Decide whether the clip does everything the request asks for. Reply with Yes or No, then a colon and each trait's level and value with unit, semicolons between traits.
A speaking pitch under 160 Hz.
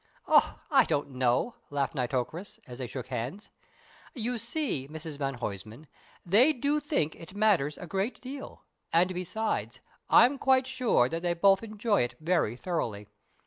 No: medium, 170 Hz